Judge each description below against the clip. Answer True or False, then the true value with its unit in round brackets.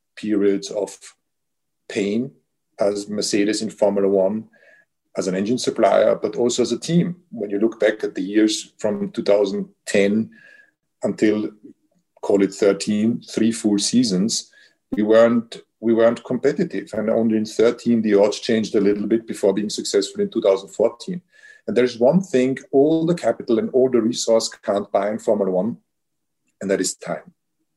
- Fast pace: False (160 wpm)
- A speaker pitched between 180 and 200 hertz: False (115 Hz)